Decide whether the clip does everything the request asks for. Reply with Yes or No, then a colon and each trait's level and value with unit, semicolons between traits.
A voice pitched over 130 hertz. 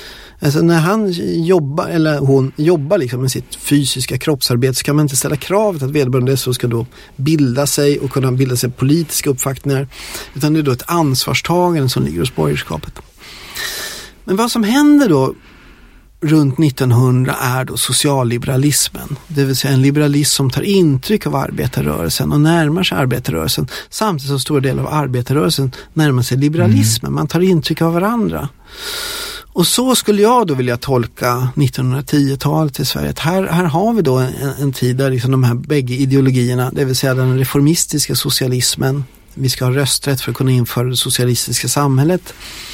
Yes: medium, 140 Hz